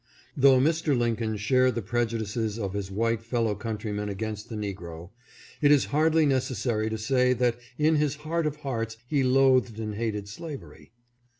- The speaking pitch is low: Yes, low, 115 Hz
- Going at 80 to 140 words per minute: No, average, 165 wpm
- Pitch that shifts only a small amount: No, average, 4.1 semitones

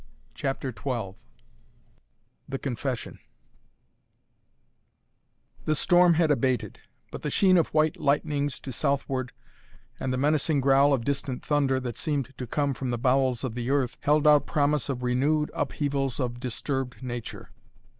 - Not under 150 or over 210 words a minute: No, average, 140 wpm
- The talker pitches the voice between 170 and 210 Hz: No, low, 135 Hz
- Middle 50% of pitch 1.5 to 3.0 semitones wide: Yes, narrow, 2.6 semitones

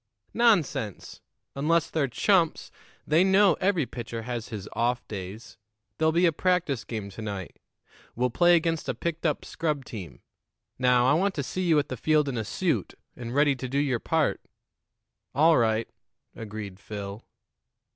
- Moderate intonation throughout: No, wide, 6.4 semitones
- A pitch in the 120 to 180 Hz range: Yes, low, 135 Hz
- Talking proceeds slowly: No, average, 165 wpm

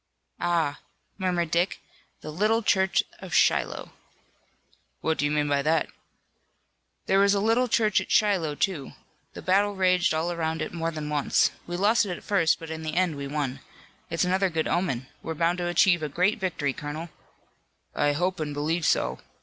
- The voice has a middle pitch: Yes, medium, 170 Hz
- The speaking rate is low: No, average, 180 wpm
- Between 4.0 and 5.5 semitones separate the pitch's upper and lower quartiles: No, average, 3.6 semitones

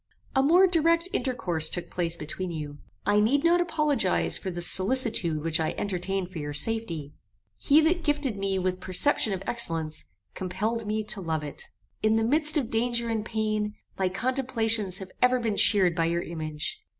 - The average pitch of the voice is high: Yes, high, 210 Hz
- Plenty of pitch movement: Yes, wide, 6.3 semitones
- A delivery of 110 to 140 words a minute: No, average, 175 wpm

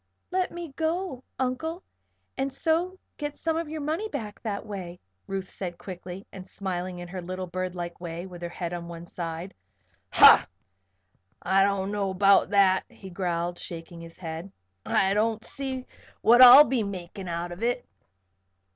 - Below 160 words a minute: No, average, 165 wpm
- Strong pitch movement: Yes, wide, 6.4 semitones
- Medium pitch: No, high, 195 Hz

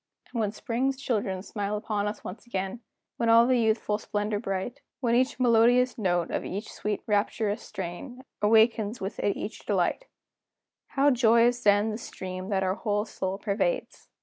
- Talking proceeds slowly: No, average, 165 wpm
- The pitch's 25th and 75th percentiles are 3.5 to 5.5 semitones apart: No, average, 2.9 semitones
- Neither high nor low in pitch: No, high, 215 Hz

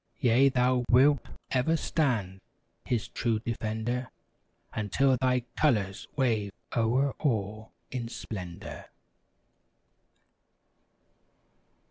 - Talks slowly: Yes, slow, 80 wpm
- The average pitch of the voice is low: Yes, low, 120 Hz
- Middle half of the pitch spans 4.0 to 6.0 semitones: No, average, 3.1 semitones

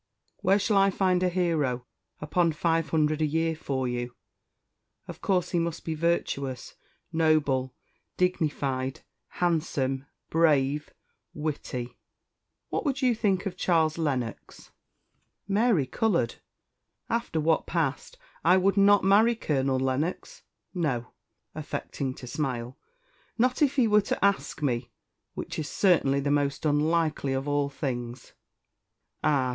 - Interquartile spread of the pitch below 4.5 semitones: No, average, 5.2 semitones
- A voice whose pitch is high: No, medium, 155 Hz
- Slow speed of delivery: Yes, slow, 130 wpm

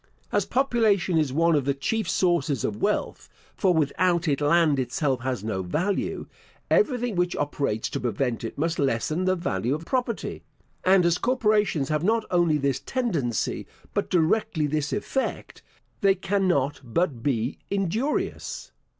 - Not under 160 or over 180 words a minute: No, average, 150 wpm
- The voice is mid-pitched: Yes, medium, 165 Hz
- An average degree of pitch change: No, wide, 6.0 semitones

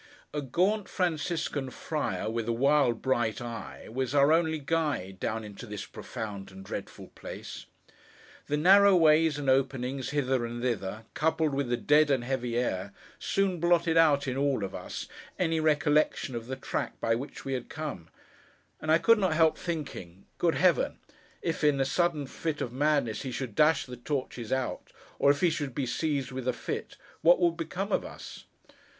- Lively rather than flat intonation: No, average, 4.9 semitones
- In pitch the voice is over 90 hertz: Yes, medium, 140 Hz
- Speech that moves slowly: No, average, 180 wpm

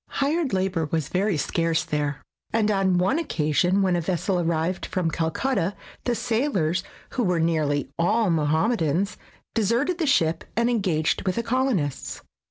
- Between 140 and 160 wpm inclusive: Yes, average, 150 wpm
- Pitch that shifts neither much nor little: No, wide, 5.9 semitones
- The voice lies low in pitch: No, medium, 185 Hz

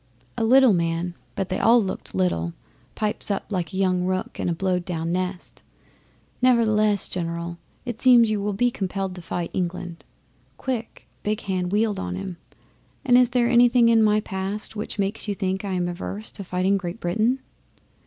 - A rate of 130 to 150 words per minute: No, average, 180 wpm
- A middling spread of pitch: Yes, average, 3.7 semitones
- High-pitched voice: Yes, high, 195 Hz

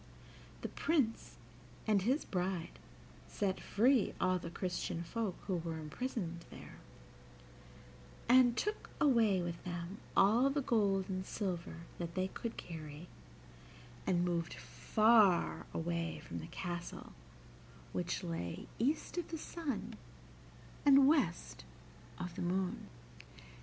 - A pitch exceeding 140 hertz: Yes, high, 190 Hz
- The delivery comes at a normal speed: No, slow, 120 wpm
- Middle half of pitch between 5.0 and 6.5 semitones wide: Yes, wide, 5.4 semitones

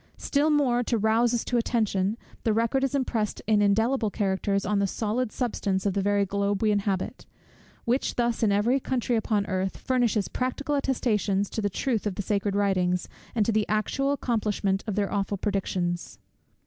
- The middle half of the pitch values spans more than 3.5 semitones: No, average, 3.2 semitones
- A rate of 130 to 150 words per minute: No, average, 180 wpm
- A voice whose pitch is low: No, high, 210 Hz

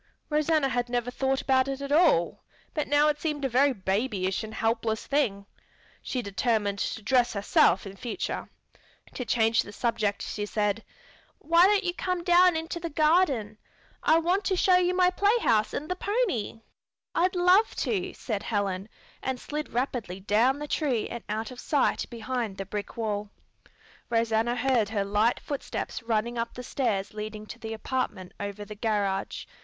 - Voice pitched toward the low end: No, high, 240 Hz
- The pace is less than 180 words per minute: Yes, average, 170 wpm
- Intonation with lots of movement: Yes, wide, 6.2 semitones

